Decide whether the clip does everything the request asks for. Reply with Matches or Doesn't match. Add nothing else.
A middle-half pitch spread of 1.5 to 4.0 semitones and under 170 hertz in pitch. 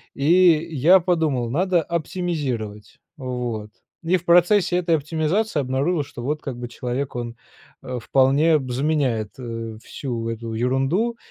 Doesn't match